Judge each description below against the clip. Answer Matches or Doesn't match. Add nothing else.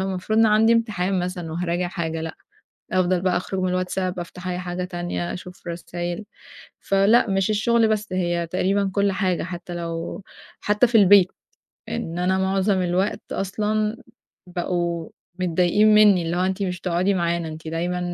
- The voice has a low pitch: Doesn't match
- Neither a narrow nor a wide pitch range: Doesn't match